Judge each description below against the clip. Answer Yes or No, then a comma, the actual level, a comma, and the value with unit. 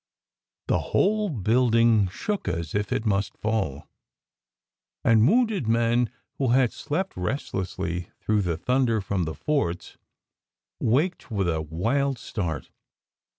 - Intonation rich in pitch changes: Yes, wide, 6.3 semitones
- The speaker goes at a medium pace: No, slow, 120 wpm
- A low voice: Yes, low, 110 Hz